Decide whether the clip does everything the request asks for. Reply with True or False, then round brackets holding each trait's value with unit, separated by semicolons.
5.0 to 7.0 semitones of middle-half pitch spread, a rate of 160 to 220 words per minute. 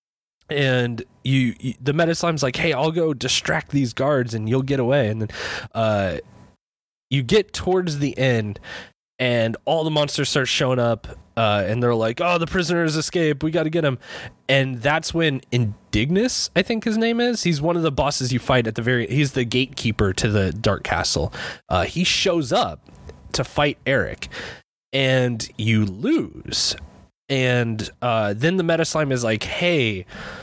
True (5.6 semitones; 175 wpm)